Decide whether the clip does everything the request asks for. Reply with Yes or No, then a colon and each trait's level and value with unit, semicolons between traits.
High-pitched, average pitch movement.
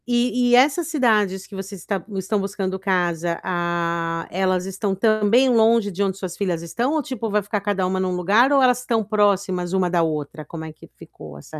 Yes: high, 195 Hz; average, 4.0 semitones